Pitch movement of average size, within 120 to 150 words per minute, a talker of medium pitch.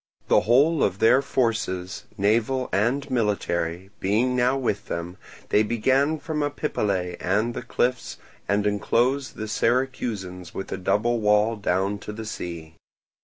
No: average, 4.5 semitones; average, 140 wpm; low, 110 Hz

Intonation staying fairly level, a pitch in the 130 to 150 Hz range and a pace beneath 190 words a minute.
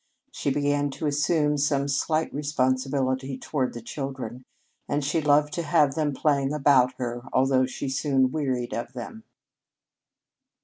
Yes: narrow, 2.2 semitones; medium, 140 Hz; average, 140 wpm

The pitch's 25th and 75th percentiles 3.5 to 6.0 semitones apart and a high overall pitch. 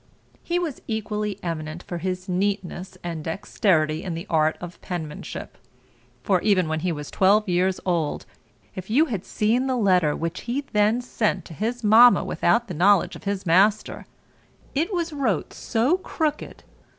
Yes: average, 4.7 semitones; high, 195 Hz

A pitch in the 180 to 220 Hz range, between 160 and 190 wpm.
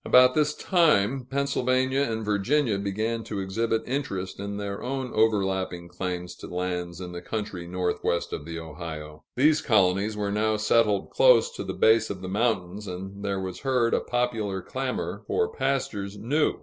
No: low, 105 Hz; average, 165 wpm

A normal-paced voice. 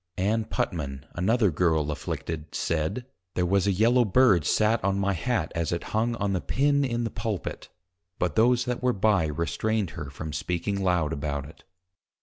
Yes: average, 180 wpm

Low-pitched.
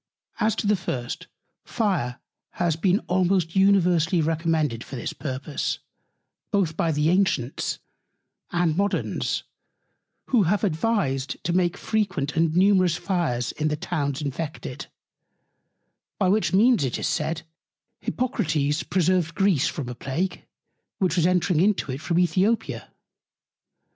No: medium, 170 Hz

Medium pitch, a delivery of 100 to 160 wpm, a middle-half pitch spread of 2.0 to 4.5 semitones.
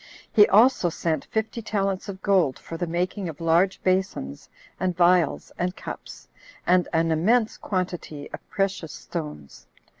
Yes: medium, 180 Hz; average, 145 wpm; average, 3.1 semitones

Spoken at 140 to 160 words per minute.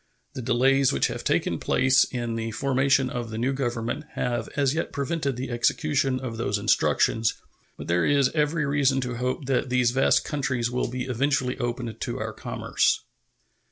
No: average, 175 wpm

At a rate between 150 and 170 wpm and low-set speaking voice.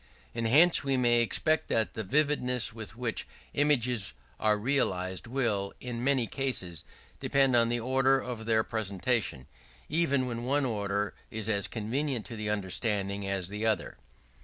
Yes: average, 155 wpm; low, 115 Hz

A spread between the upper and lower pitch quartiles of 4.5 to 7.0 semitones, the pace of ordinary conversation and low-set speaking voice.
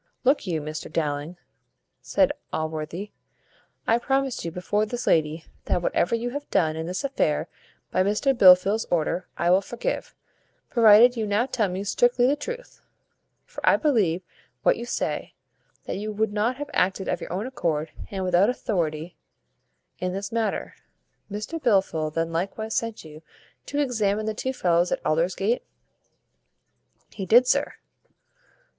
No: wide, 5.6 semitones; average, 150 wpm; high, 200 Hz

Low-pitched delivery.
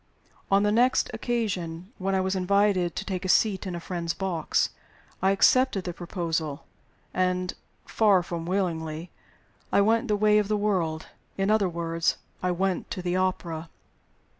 No: medium, 185 Hz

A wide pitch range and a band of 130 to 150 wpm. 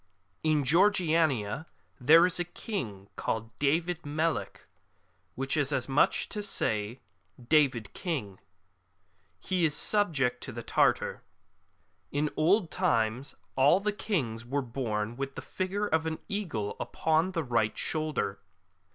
Yes: wide, 6.2 semitones; average, 140 wpm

